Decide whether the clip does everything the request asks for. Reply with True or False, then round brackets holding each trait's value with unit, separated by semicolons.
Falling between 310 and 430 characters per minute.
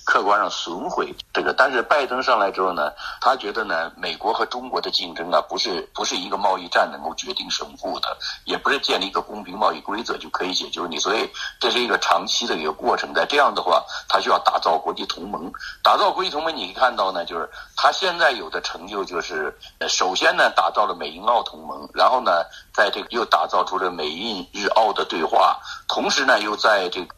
True (325 characters per minute)